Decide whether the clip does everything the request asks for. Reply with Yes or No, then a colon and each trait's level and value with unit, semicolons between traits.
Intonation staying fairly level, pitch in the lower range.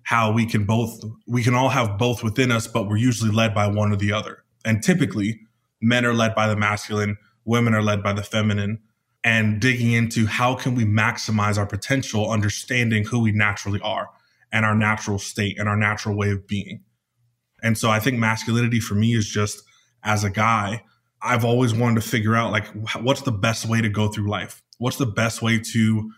Yes: narrow, 1.9 semitones; low, 110 Hz